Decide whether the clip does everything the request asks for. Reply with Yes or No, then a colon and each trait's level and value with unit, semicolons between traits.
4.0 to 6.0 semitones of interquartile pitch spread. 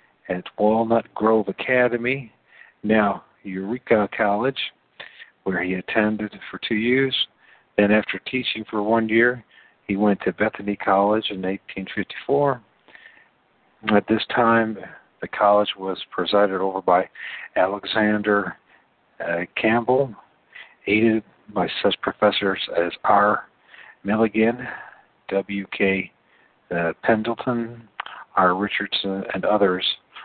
No: narrow, 2.6 semitones